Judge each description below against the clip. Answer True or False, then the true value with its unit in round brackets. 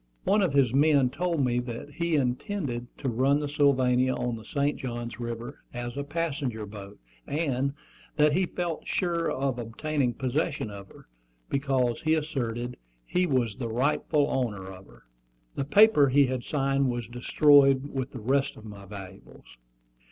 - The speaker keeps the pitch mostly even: False (3.5 semitones)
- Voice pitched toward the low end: True (130 Hz)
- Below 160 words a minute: False (165 wpm)